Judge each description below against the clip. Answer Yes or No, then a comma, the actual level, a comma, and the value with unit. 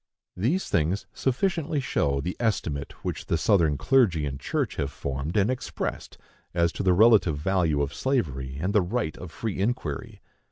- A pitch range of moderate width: No, wide, 7.6 semitones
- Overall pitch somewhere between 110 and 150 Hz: No, very low, 90 Hz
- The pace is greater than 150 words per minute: Yes, average, 165 wpm